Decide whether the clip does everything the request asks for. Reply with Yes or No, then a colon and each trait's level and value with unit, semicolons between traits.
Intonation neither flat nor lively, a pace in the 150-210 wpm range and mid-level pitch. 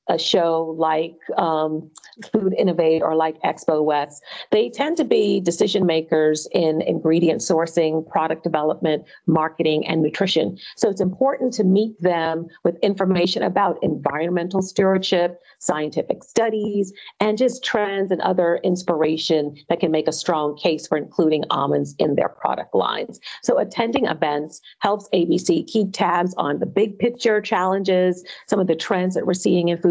Yes: average, 3.9 semitones; average, 155 wpm; medium, 175 Hz